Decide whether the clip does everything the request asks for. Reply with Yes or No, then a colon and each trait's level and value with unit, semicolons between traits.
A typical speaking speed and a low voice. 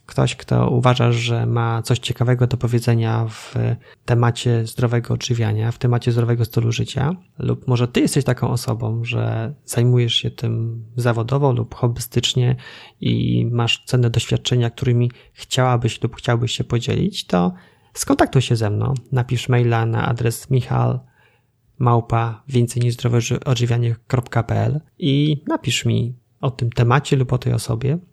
Yes: average, 130 wpm; low, 120 Hz